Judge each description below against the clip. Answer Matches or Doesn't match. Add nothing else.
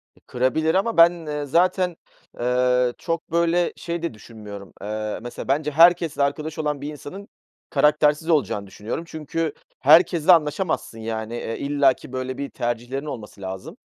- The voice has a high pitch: Doesn't match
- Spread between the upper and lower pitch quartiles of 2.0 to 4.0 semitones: Doesn't match